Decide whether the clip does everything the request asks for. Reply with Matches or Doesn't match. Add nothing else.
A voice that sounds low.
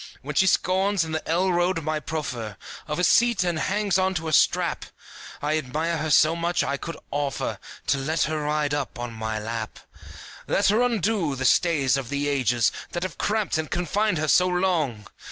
Doesn't match